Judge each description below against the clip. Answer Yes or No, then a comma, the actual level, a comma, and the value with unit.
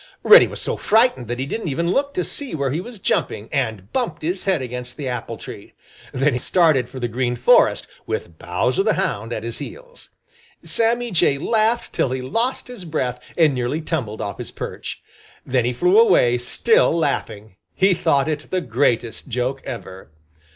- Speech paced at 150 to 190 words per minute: Yes, average, 185 wpm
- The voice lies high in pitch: No, medium, 140 Hz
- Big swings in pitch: Yes, wide, 7.7 semitones